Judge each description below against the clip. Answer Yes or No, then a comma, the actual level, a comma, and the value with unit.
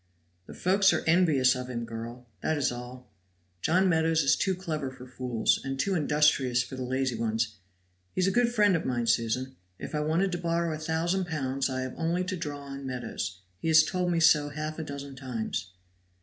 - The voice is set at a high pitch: No, medium, 140 Hz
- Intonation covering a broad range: No, average, 4.6 semitones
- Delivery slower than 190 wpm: No, fast, 205 wpm